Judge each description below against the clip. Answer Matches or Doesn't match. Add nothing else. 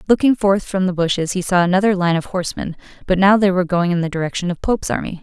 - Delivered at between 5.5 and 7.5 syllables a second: Matches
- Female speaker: Matches